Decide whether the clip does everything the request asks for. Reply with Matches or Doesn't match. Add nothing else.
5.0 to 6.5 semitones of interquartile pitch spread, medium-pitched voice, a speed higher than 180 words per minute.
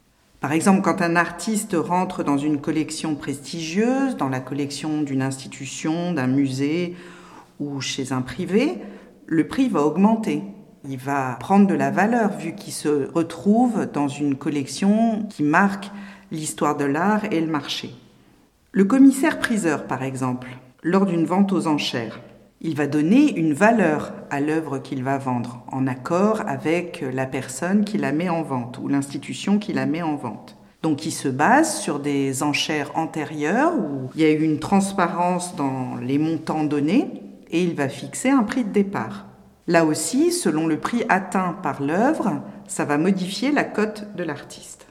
Doesn't match